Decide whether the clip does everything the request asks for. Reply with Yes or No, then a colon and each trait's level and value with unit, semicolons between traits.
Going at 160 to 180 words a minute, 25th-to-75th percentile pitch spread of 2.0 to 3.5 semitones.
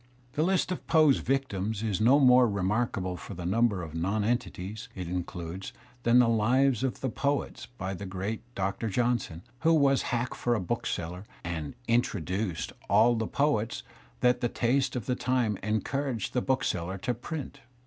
No: average, 170 wpm; average, 5.0 semitones